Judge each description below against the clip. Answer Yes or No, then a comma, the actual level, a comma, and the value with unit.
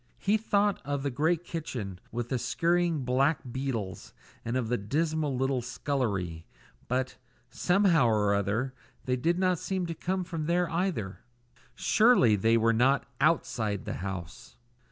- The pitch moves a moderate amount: No, wide, 6.7 semitones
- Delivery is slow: No, average, 150 wpm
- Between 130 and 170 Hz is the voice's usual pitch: Yes, low, 135 Hz